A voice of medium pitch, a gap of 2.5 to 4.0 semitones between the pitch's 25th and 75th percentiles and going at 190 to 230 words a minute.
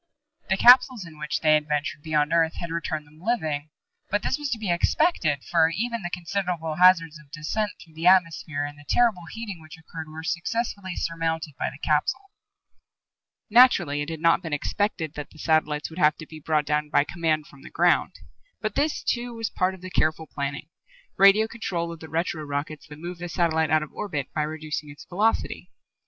Yes: medium, 165 Hz; average, 3.6 semitones; average, 200 wpm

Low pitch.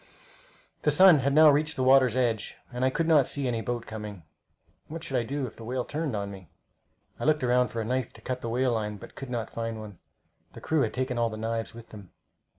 Yes: low, 125 Hz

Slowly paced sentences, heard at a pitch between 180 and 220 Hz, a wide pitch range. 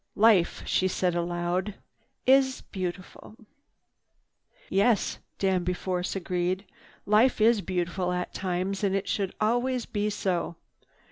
No: slow, 110 wpm; high, 190 Hz; average, 2.9 semitones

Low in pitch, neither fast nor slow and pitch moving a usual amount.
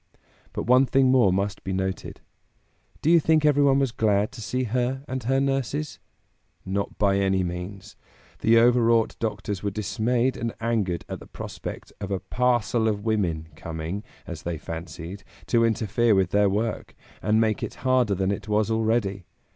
Yes: low, 110 Hz; average, 170 wpm; average, 4.0 semitones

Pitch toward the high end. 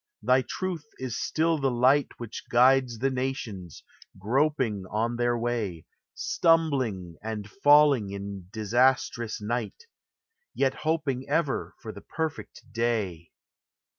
No: low, 120 Hz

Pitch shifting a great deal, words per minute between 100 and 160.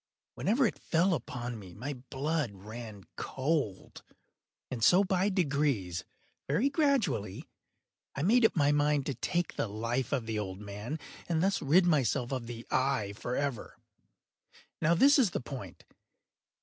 Yes: wide, 6.9 semitones; average, 140 wpm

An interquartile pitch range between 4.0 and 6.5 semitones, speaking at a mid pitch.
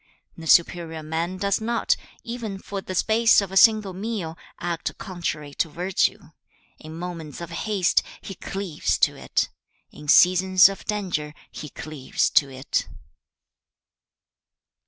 No: average, 3.6 semitones; medium, 180 Hz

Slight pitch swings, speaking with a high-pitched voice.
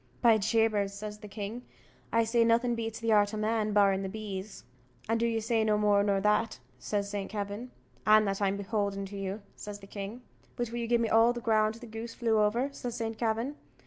Yes: narrow, 2.1 semitones; high, 215 Hz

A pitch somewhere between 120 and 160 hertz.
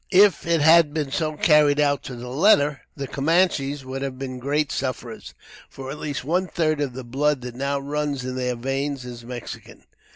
Yes: medium, 140 Hz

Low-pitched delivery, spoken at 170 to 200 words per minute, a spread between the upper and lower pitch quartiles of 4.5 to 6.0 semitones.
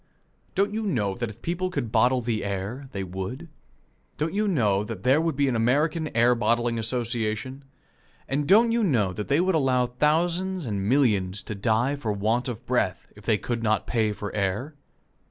Yes: low, 120 Hz; average, 190 wpm; wide, 5.6 semitones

